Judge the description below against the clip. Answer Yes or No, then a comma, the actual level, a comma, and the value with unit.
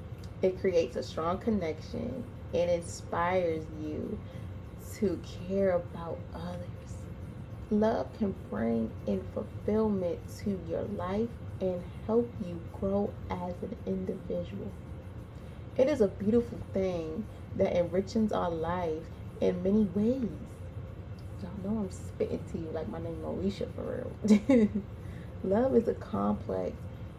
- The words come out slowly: Yes, slow, 120 wpm